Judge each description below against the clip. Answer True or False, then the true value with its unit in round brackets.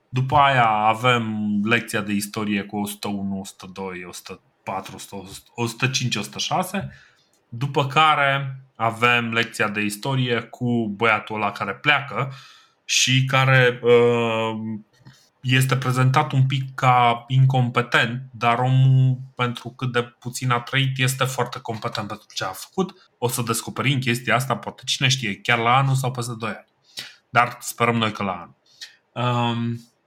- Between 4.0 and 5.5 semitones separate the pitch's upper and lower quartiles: False (2.9 semitones)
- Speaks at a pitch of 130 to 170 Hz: False (120 Hz)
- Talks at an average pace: True (135 wpm)